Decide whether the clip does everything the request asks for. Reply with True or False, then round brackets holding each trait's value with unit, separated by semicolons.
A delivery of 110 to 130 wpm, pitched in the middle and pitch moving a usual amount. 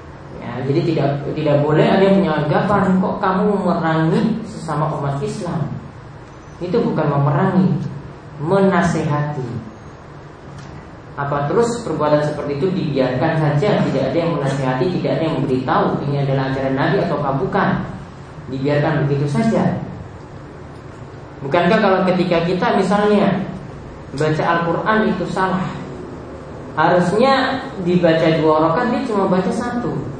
True (120 wpm; 160 Hz; 4.9 semitones)